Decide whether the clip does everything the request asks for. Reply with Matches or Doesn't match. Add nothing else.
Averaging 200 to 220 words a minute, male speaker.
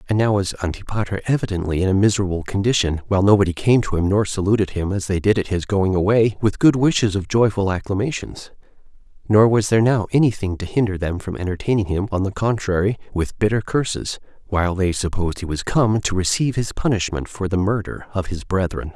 Matches